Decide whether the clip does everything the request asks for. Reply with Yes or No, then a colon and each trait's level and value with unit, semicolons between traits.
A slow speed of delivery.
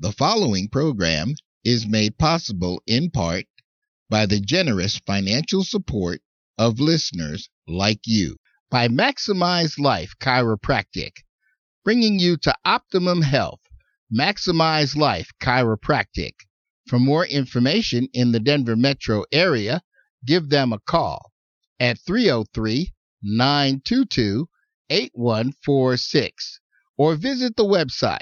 Yes: slow, 100 wpm